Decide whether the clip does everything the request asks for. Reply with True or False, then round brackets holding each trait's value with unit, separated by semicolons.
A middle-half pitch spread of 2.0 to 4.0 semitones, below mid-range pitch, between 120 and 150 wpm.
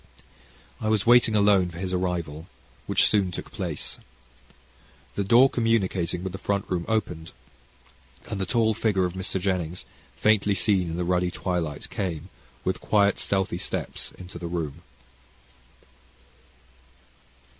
True (2.7 semitones; 95 Hz; 135 wpm)